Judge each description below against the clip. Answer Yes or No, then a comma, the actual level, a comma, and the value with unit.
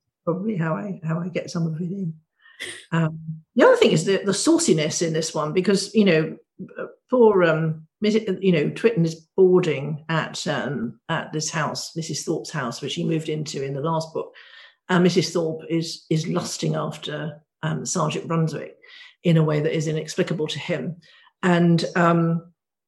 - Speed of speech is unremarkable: Yes, average, 180 wpm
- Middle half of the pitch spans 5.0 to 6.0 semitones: No, average, 2.7 semitones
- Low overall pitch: No, medium, 165 Hz